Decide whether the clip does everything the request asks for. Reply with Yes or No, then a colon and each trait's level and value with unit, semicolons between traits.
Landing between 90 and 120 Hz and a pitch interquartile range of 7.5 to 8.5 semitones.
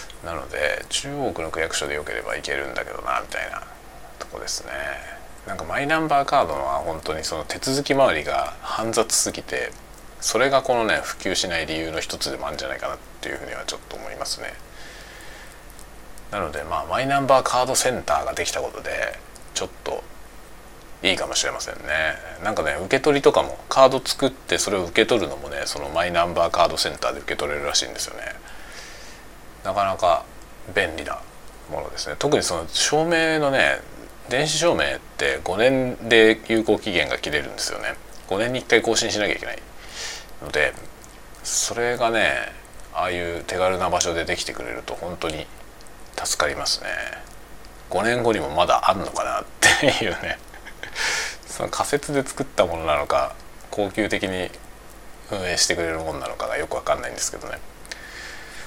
Yes: low, 110 Hz; wide, 7.9 semitones